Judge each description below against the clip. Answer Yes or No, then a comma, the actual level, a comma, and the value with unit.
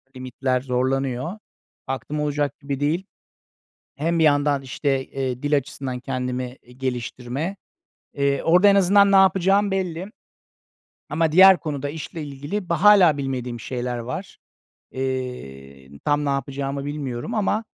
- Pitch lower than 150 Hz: Yes, medium, 140 Hz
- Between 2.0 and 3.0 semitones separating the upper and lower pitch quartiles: No, average, 4.5 semitones